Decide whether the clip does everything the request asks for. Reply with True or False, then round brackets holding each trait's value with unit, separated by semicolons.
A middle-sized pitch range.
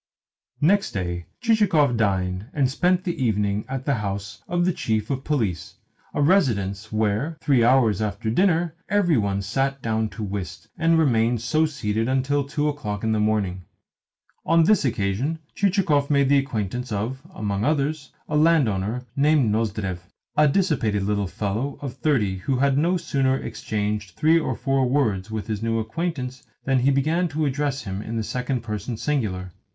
False (5.8 semitones)